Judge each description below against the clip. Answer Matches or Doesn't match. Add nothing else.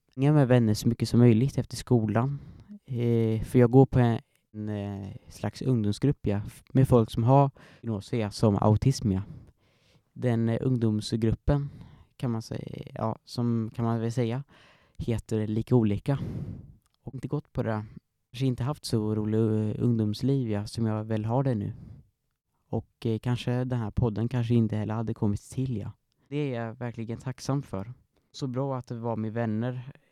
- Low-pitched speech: Matches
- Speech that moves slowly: Doesn't match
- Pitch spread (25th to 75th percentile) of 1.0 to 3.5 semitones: Matches